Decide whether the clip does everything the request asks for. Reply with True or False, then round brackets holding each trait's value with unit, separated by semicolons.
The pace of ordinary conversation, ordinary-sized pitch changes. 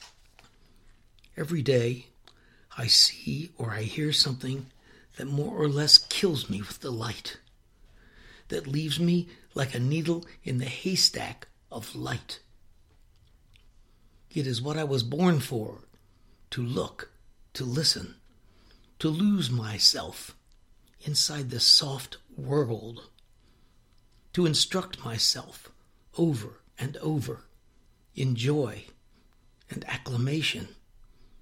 False (105 wpm; 4.7 semitones)